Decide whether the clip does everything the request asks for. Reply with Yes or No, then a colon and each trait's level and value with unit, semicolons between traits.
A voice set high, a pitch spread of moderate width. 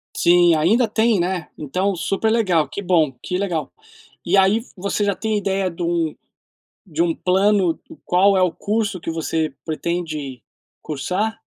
No: medium, 180 Hz; average, 3.5 semitones